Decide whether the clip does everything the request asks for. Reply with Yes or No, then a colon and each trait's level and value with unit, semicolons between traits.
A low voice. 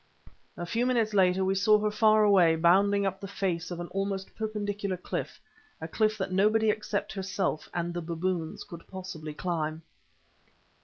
No: high, 195 Hz